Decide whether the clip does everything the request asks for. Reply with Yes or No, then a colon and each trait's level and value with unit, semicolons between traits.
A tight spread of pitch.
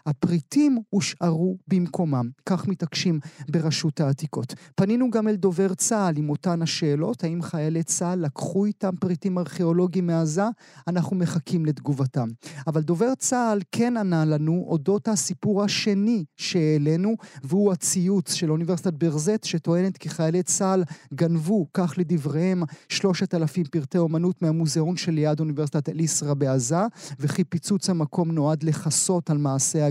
No: average, 3.4 semitones